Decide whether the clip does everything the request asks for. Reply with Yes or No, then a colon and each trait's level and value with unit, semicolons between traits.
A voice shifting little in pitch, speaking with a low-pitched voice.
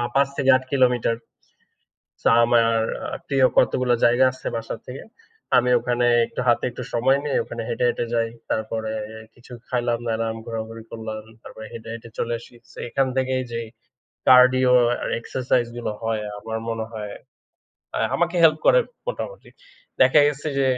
Yes: narrow, 2.3 semitones; low, 120 Hz